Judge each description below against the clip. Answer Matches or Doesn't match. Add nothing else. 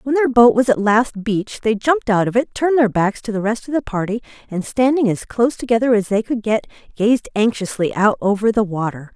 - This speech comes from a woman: Matches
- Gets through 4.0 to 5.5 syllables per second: Doesn't match